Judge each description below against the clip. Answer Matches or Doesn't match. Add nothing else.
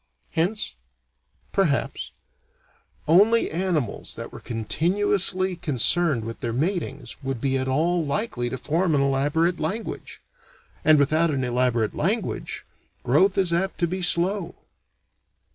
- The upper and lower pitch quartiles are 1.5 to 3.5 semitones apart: Doesn't match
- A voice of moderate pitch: Matches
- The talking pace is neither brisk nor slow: Doesn't match